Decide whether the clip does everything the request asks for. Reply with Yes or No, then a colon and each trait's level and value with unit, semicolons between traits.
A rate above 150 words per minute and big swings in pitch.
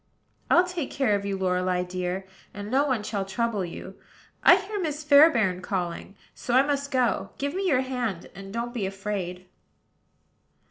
Yes: average, 170 wpm; wide, 6.6 semitones